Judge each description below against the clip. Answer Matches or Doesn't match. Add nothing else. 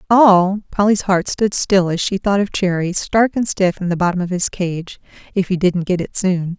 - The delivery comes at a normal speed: Doesn't match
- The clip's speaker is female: Matches